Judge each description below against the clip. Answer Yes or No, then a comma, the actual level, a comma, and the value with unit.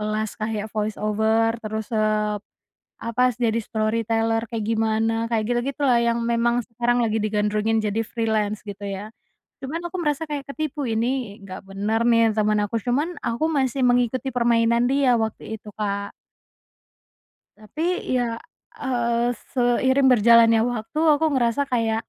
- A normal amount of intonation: No, narrow, 2.2 semitones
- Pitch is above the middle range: Yes, high, 230 Hz